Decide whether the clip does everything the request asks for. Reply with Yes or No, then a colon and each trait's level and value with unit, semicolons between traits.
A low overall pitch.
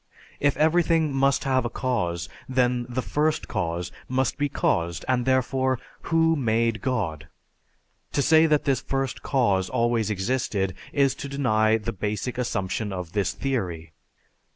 Yes: low, 125 Hz